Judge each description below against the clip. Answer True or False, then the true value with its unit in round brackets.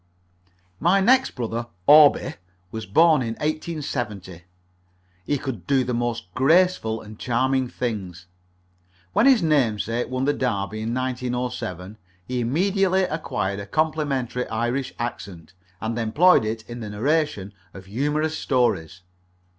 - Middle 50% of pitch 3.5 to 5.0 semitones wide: False (5.5 semitones)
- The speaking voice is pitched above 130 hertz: False (125 Hz)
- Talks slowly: True (125 wpm)